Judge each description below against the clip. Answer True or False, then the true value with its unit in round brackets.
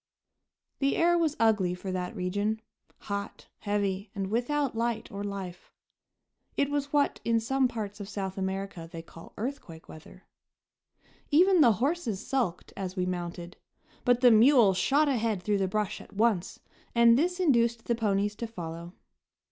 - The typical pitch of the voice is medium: False (215 Hz)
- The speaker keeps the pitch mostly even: False (4.6 semitones)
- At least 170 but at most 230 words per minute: False (155 wpm)